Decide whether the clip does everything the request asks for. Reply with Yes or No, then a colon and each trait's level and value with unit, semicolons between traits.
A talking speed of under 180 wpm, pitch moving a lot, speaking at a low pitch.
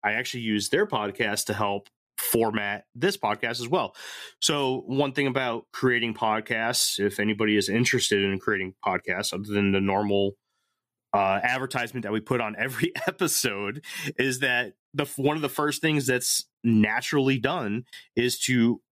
No: average, 160 wpm; average, 4.2 semitones; low, 120 Hz